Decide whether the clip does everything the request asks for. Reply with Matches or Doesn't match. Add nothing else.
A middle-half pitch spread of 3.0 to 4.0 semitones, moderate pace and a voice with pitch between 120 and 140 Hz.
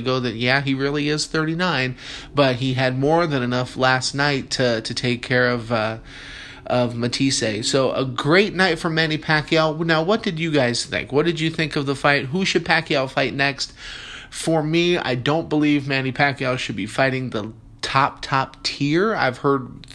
Matches